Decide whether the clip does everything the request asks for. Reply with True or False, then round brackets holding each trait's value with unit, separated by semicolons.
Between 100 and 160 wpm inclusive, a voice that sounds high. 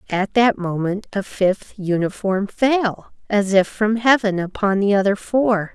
True (155 wpm; 205 Hz)